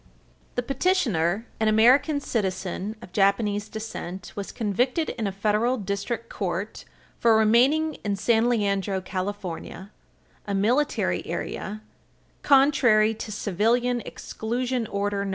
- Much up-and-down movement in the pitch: No, average, 3.4 semitones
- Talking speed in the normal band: No, slow, 115 wpm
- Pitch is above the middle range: Yes, high, 215 Hz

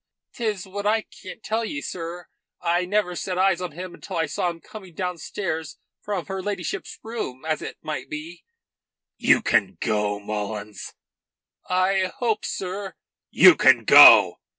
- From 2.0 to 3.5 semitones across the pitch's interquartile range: No, average, 3.9 semitones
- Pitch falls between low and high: Yes, medium, 180 Hz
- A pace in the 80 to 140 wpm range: No, average, 155 wpm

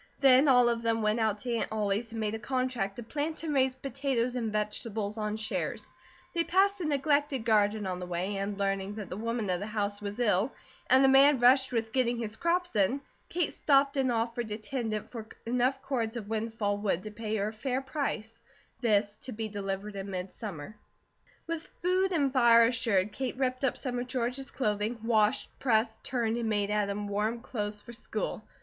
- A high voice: Yes, high, 230 Hz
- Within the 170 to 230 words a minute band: Yes, average, 185 wpm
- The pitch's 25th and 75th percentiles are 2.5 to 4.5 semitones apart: Yes, average, 3.7 semitones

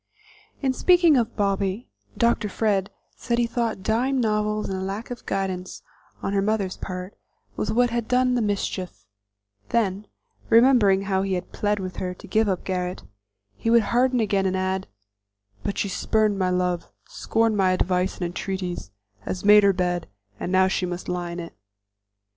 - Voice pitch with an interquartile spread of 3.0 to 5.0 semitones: Yes, average, 3.4 semitones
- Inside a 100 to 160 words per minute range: No, average, 170 wpm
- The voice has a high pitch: Yes, high, 195 Hz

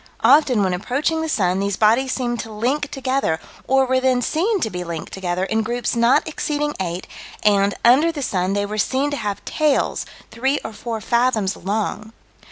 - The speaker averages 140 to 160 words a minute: No, average, 185 wpm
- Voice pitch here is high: Yes, high, 235 Hz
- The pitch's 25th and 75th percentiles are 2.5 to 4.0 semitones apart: No, average, 5.0 semitones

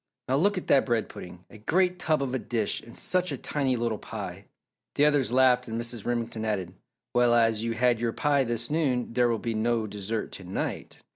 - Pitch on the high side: No, low, 120 Hz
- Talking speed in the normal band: No, fast, 215 wpm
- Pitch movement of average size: Yes, average, 3.0 semitones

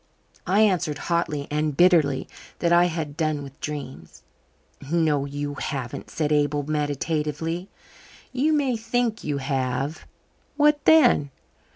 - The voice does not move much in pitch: No, average, 3.7 semitones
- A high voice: No, medium, 155 Hz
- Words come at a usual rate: No, slow, 125 wpm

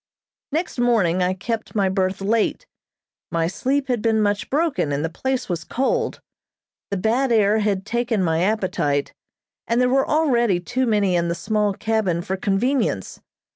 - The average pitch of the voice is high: Yes, high, 210 Hz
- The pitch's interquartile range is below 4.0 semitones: No, average, 4.7 semitones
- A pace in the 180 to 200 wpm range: No, average, 165 wpm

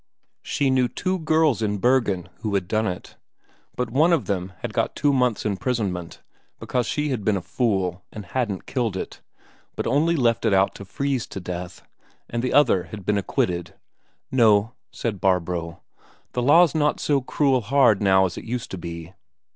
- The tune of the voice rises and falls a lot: Yes, wide, 5.7 semitones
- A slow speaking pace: No, average, 180 wpm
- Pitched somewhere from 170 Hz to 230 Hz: No, low, 110 Hz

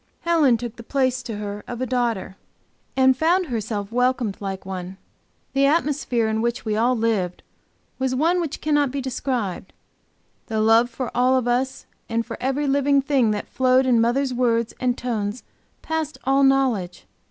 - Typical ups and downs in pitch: Yes, average, 3.3 semitones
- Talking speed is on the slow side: No, average, 170 wpm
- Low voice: No, very high, 250 Hz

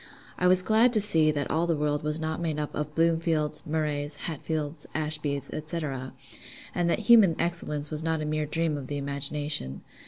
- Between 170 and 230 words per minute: Yes, average, 185 wpm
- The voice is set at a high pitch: No, medium, 155 Hz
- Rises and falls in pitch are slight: Yes, narrow, 2.2 semitones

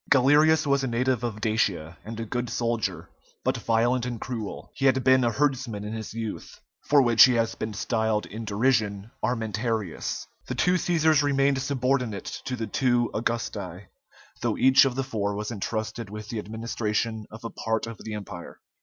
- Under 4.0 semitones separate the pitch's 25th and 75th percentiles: Yes, average, 3.3 semitones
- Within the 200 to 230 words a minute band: No, average, 180 wpm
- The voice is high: No, low, 115 Hz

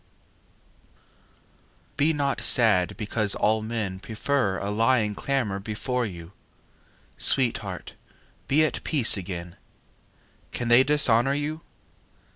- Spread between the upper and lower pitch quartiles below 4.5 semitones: No, average, 5.3 semitones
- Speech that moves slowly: Yes, slow, 105 wpm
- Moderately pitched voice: No, low, 115 Hz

